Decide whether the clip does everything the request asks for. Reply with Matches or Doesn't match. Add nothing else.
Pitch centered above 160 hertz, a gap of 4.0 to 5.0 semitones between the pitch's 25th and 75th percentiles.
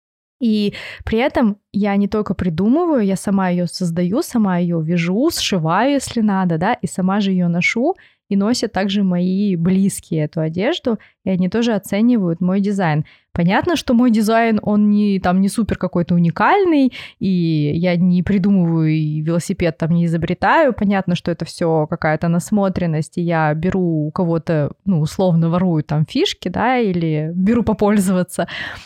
Doesn't match